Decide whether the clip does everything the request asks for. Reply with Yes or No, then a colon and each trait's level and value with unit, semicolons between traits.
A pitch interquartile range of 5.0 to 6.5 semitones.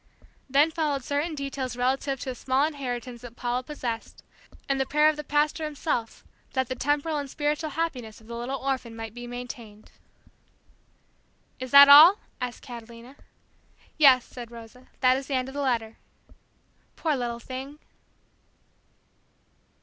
No: average, 3.1 semitones